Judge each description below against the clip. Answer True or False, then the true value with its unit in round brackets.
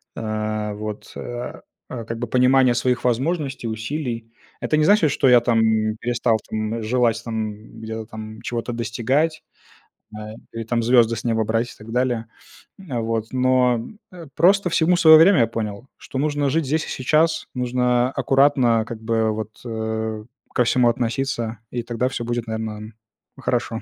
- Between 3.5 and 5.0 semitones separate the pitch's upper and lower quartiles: False (2.7 semitones)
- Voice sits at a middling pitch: False (120 Hz)